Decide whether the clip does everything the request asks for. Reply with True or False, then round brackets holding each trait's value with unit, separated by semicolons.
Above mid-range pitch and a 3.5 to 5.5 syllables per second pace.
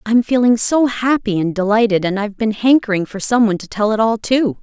False (220 Hz; 5.8 syllables/s)